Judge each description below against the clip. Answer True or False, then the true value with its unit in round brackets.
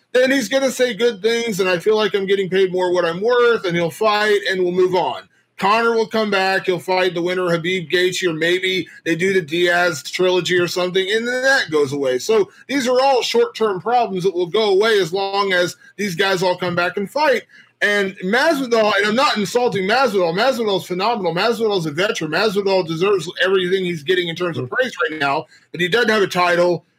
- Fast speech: True (225 wpm)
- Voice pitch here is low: False (195 Hz)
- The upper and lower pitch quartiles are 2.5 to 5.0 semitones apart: True (4.0 semitones)